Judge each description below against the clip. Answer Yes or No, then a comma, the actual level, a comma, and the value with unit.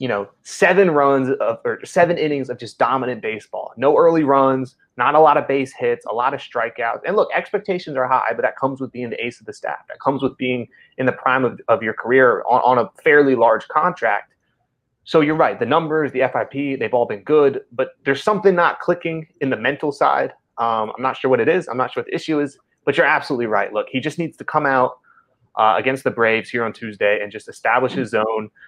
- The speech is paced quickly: Yes, fast, 240 wpm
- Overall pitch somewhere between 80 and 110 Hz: No, low, 135 Hz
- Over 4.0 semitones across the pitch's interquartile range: Yes, average, 4.4 semitones